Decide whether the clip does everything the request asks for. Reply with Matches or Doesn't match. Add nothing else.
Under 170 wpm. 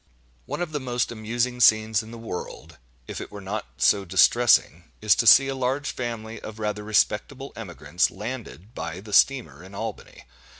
Doesn't match